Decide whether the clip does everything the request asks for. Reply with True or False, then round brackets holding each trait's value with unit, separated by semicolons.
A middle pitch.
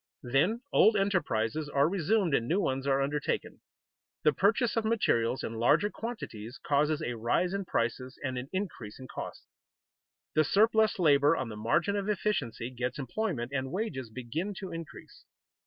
True (145 Hz)